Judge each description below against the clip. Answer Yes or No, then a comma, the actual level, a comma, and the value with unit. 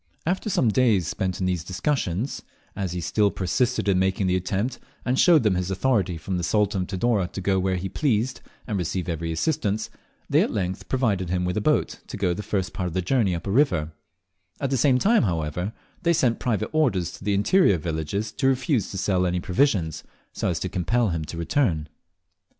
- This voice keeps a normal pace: No, fast, 210 wpm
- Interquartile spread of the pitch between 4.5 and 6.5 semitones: Yes, average, 5.3 semitones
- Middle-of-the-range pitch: No, very low, 95 Hz